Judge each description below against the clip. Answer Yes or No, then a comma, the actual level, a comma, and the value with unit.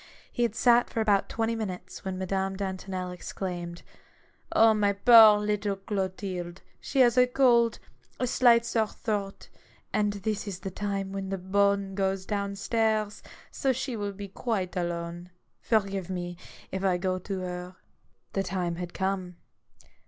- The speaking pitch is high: Yes, high, 195 Hz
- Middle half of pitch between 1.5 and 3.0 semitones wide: Yes, narrow, 2.6 semitones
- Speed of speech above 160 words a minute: No, average, 155 wpm